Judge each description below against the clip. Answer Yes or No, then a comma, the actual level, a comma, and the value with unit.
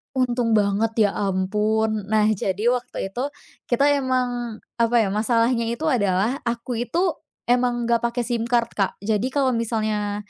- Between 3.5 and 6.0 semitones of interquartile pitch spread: No, narrow, 2.5 semitones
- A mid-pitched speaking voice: No, high, 230 Hz